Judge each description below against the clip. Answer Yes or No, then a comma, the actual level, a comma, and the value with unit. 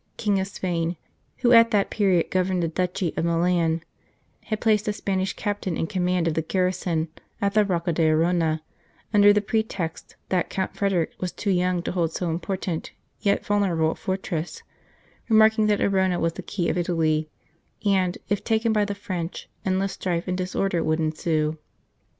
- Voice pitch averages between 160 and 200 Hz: Yes, medium, 185 Hz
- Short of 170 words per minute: No, average, 175 wpm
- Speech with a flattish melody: No, average, 3.2 semitones